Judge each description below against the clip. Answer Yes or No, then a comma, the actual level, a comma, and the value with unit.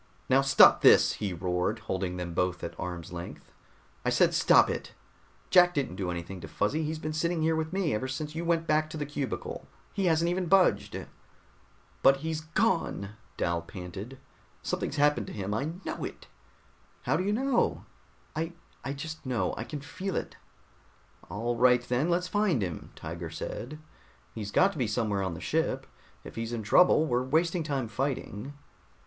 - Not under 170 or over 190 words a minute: Yes, average, 180 wpm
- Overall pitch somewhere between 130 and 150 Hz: Yes, low, 135 Hz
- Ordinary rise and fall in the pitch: No, wide, 8.1 semitones